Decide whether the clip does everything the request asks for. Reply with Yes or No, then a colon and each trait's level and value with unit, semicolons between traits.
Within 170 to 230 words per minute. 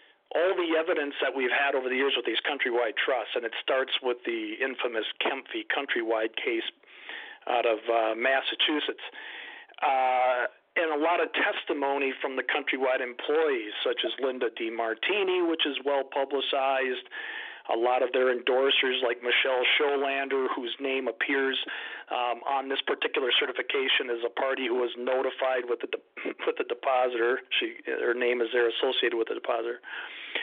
No: average, 160 wpm